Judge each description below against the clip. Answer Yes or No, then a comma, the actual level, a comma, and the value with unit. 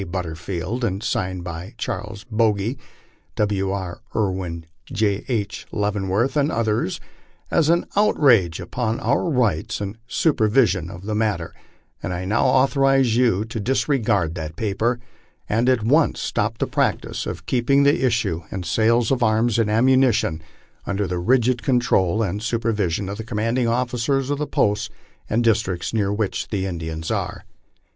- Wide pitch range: No, average, 4.2 semitones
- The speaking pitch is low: Yes, low, 110 Hz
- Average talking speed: Yes, average, 150 wpm